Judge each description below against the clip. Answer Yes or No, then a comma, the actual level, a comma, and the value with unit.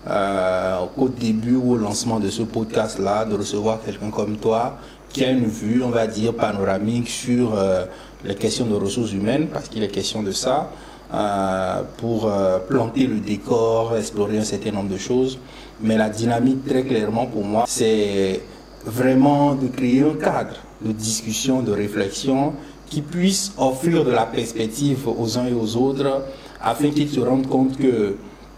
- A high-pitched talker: No, low, 115 Hz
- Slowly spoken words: No, average, 170 wpm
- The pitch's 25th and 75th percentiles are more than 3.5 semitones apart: Yes, average, 3.9 semitones